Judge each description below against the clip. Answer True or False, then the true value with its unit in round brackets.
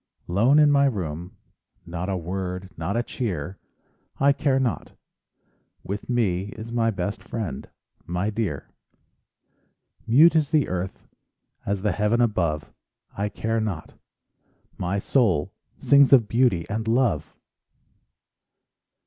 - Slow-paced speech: True (115 wpm)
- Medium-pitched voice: False (105 Hz)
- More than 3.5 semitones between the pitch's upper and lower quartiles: True (5.1 semitones)